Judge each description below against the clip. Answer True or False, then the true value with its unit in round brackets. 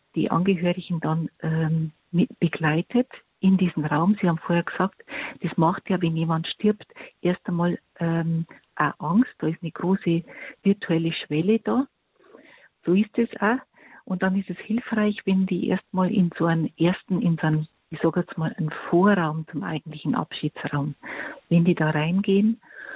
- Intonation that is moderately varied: True (3.3 semitones)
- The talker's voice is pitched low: False (175 Hz)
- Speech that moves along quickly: False (165 wpm)